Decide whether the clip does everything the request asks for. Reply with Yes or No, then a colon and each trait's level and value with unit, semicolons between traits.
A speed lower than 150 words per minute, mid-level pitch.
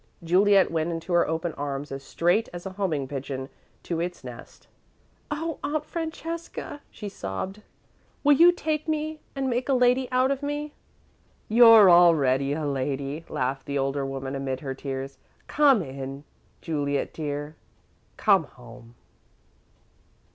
Yes: average, 140 wpm; medium, 170 Hz